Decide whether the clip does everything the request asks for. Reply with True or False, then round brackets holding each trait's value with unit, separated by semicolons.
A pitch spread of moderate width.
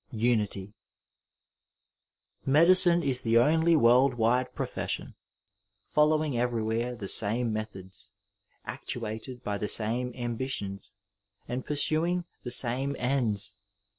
True (3.9 semitones)